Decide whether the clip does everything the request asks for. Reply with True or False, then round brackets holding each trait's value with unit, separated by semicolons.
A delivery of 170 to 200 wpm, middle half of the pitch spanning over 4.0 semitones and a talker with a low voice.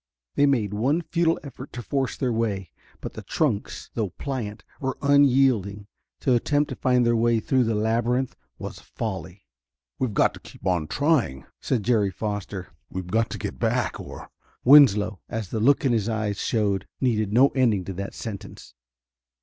True (175 wpm; 4.4 semitones; 115 Hz)